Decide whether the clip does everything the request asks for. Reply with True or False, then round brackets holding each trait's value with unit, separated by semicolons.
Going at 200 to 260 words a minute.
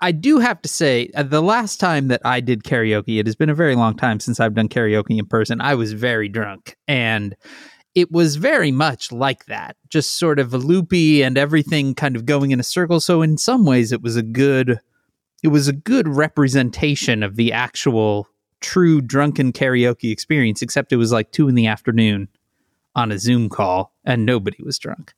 True (205 wpm)